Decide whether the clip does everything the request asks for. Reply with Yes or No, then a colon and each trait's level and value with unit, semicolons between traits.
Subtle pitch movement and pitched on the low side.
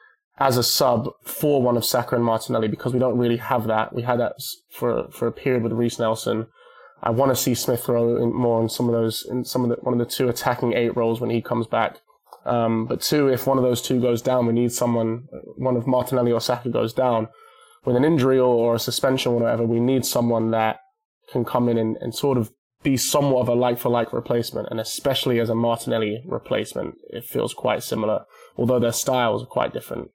Yes: narrow, 1.7 semitones; low, 120 Hz